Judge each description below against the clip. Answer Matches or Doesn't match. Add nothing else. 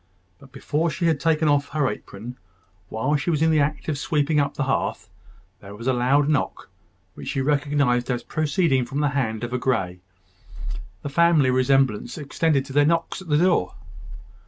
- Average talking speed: Matches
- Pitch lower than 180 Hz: Matches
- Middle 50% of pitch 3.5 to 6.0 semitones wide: Doesn't match